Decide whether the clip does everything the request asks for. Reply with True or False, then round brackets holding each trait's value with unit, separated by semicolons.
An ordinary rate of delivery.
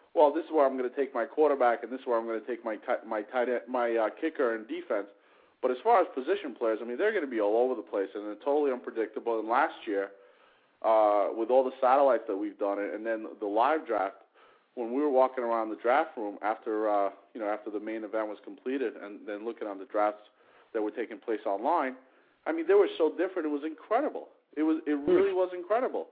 False (250 wpm)